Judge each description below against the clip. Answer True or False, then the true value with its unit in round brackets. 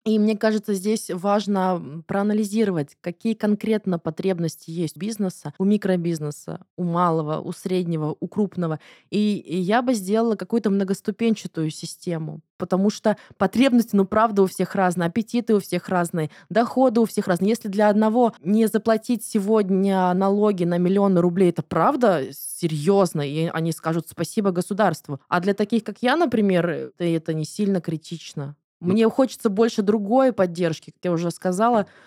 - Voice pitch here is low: False (190 Hz)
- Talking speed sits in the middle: True (150 wpm)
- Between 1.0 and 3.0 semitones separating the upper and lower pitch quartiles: False (4.1 semitones)